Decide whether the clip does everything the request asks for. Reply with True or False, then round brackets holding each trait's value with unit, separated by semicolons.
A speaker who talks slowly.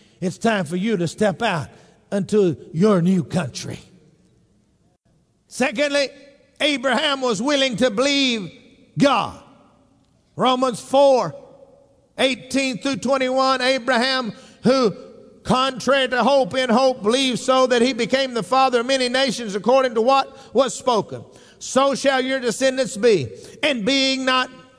True (130 wpm)